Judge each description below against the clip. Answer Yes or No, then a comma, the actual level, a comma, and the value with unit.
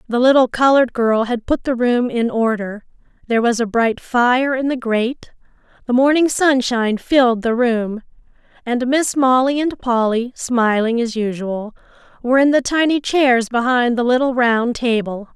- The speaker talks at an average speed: Yes, average, 165 wpm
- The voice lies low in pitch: No, high, 245 Hz